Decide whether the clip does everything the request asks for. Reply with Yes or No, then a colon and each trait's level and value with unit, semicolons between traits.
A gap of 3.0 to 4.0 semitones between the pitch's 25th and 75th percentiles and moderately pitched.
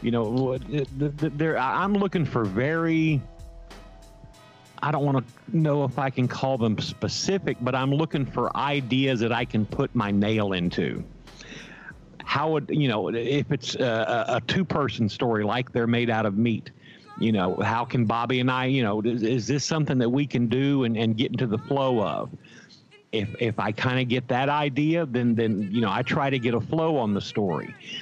No: average, 3.5 semitones; low, 125 Hz